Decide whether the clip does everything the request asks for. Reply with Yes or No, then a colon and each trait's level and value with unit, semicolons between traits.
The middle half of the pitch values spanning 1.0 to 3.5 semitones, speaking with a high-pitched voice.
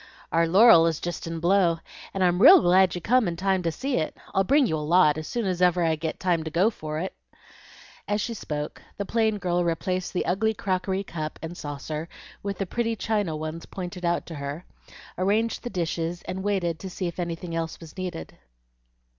No: average, 3.0 semitones; medium, 180 Hz